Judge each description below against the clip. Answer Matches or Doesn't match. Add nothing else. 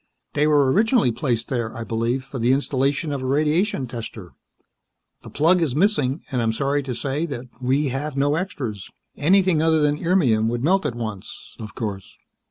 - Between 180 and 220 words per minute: Matches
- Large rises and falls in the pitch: Doesn't match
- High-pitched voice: Doesn't match